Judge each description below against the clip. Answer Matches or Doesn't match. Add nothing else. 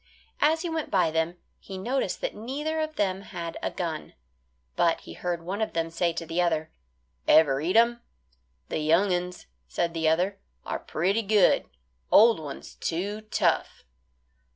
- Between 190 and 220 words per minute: Doesn't match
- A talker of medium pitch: Matches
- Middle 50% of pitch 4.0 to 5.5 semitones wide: Matches